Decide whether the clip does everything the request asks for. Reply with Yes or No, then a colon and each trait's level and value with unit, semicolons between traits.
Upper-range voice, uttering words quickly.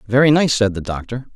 No: low, 120 Hz; fast, 220 wpm